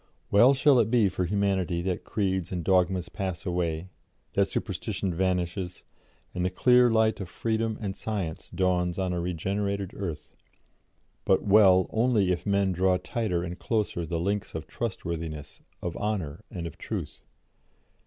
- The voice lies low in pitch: Yes, very low, 95 Hz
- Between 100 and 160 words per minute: Yes, average, 155 wpm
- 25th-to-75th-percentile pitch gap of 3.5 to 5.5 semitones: No, average, 2.8 semitones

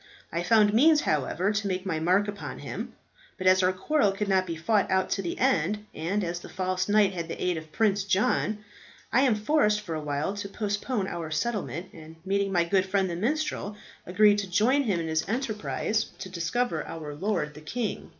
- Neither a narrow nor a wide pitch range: Yes, average, 3.5 semitones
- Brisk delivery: Yes, fast, 210 wpm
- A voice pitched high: Yes, high, 195 Hz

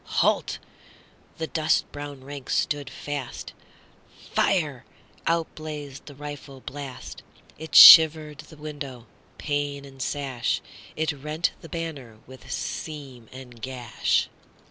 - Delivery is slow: Yes, slow, 95 wpm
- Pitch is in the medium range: Yes, medium, 145 Hz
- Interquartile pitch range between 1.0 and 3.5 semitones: Yes, narrow, 2.6 semitones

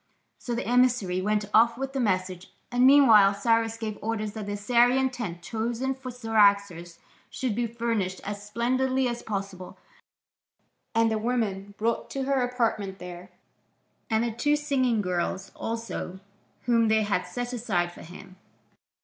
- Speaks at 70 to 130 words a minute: No, average, 150 wpm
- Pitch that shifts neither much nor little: Yes, average, 3.5 semitones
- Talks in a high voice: Yes, high, 225 Hz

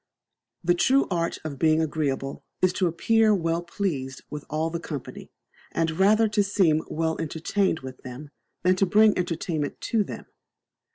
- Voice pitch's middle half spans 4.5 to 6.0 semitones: No, average, 4.0 semitones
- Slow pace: No, average, 160 wpm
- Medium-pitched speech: Yes, medium, 165 Hz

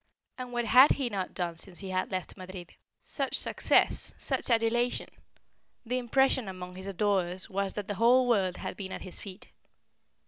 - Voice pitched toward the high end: Yes, high, 200 Hz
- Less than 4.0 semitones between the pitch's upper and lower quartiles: No, average, 4.4 semitones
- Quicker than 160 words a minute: Yes, average, 175 wpm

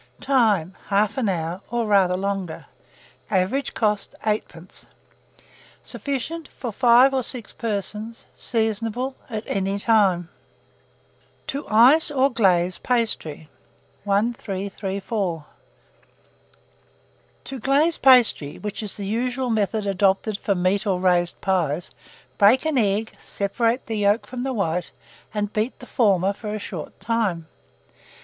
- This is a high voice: Yes, high, 210 Hz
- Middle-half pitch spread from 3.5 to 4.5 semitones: Yes, average, 3.8 semitones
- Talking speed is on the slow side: Yes, slow, 120 wpm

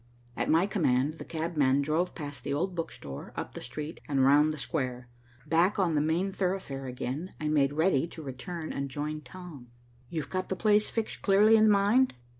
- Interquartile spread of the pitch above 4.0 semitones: Yes, average, 4.9 semitones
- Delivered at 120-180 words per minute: No, average, 195 wpm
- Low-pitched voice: No, medium, 155 Hz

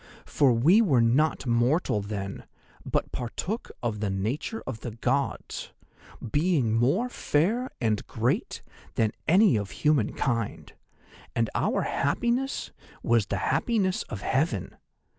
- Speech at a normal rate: No, slow, 125 wpm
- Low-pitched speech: Yes, low, 130 Hz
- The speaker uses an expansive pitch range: Yes, wide, 7.7 semitones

